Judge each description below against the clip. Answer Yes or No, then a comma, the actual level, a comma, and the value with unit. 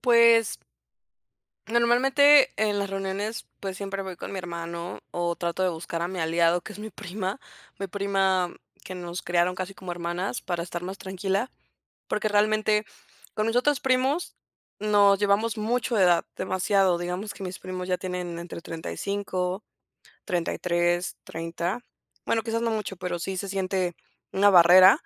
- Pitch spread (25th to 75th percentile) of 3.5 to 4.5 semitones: No, average, 3.1 semitones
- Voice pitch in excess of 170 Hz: Yes, high, 190 Hz